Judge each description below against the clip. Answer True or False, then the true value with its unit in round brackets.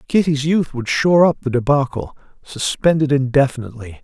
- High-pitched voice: False (140 Hz)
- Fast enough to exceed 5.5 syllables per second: True (5.7 syllables/s)